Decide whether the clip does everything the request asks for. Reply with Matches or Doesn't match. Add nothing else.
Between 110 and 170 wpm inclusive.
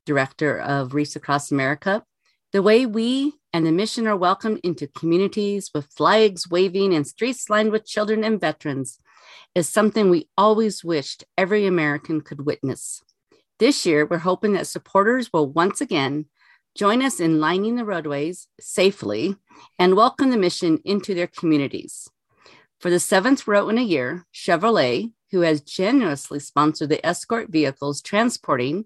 Matches